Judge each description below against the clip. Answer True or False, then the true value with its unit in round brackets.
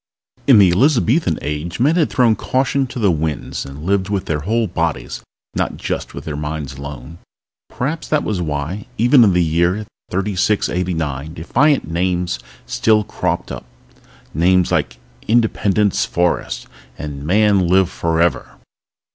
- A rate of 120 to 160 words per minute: True (140 wpm)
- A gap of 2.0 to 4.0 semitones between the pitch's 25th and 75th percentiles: False (5.3 semitones)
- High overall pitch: False (90 Hz)